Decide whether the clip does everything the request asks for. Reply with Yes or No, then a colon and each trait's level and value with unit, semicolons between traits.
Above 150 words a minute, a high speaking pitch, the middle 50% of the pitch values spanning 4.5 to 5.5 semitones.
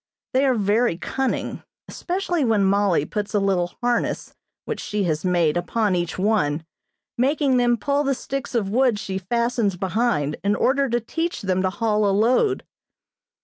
Yes: average, 165 wpm; high, 215 Hz; average, 4.9 semitones